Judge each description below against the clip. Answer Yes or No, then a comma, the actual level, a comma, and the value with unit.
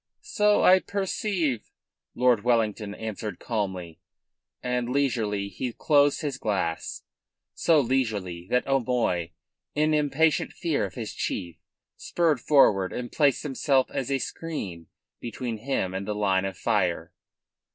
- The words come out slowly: Yes, slow, 130 wpm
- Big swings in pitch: Yes, wide, 6.0 semitones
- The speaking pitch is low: Yes, low, 120 Hz